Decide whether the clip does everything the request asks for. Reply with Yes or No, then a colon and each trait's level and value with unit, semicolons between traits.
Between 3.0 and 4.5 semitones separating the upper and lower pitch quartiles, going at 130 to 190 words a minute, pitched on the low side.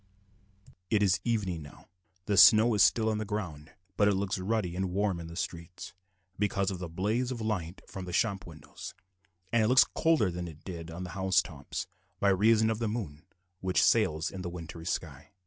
No: average, 4.0 semitones; average, 200 wpm; very low, 95 Hz